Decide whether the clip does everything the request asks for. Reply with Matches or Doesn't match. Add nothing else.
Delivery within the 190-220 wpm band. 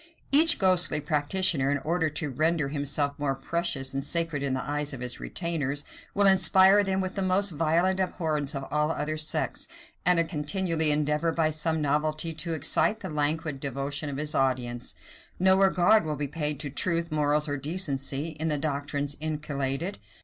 Doesn't match